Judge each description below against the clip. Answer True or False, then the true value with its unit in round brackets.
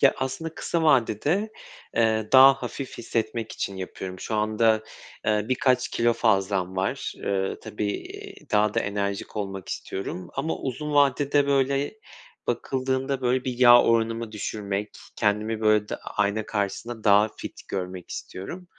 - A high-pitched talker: False (110 Hz)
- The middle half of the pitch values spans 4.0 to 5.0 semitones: True (4.3 semitones)